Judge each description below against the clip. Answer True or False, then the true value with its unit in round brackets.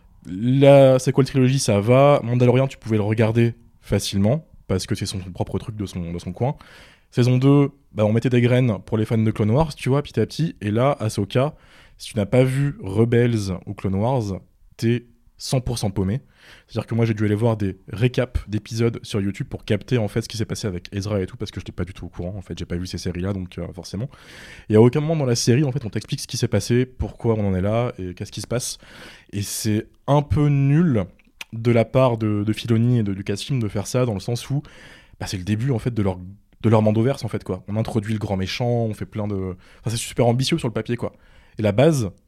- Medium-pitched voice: False (110 Hz)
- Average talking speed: False (265 wpm)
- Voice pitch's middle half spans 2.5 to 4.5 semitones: True (3.8 semitones)